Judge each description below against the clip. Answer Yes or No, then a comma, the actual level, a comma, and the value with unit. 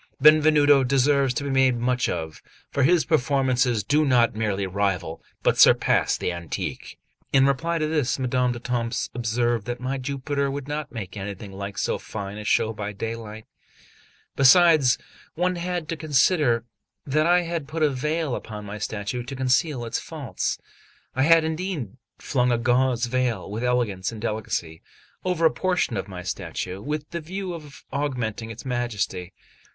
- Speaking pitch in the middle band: No, low, 125 Hz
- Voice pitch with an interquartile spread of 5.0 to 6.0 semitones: Yes, average, 5.3 semitones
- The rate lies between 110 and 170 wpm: Yes, average, 165 wpm